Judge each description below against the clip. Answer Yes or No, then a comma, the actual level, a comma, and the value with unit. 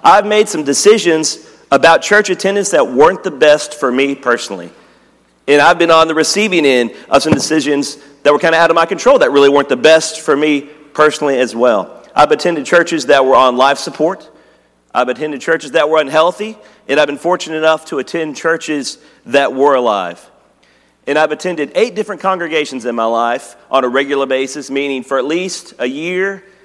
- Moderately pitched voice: Yes, medium, 150 Hz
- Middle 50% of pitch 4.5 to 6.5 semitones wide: No, average, 3.3 semitones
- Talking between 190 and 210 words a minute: Yes, average, 195 wpm